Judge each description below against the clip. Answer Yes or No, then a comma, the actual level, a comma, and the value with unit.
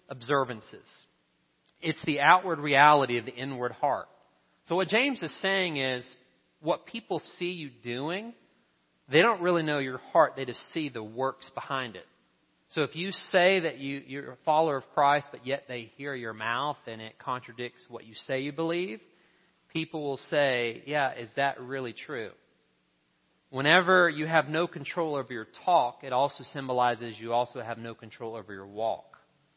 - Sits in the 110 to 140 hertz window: Yes, low, 135 Hz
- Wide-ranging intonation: No, average, 4.9 semitones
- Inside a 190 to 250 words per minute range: No, average, 175 wpm